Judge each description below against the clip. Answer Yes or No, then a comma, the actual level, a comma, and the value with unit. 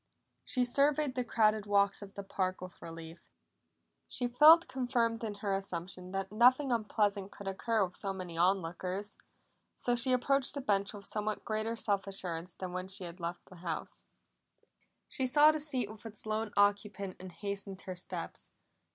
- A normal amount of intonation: Yes, average, 4.0 semitones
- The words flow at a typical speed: Yes, average, 175 wpm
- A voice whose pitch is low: No, high, 205 Hz